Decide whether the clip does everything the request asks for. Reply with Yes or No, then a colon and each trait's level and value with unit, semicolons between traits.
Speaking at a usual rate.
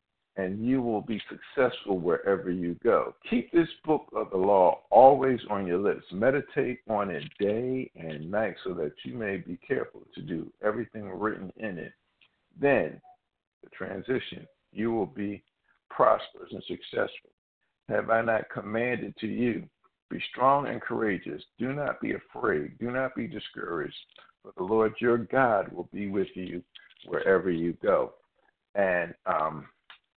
Yes: average, 155 wpm